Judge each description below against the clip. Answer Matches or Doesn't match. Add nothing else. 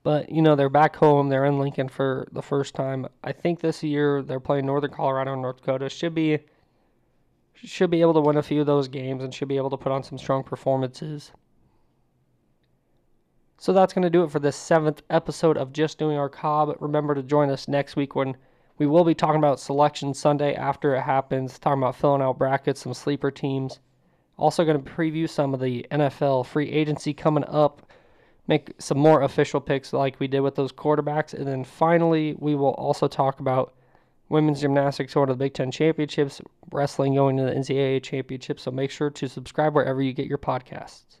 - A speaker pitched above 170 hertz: Doesn't match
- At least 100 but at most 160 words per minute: Doesn't match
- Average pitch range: Doesn't match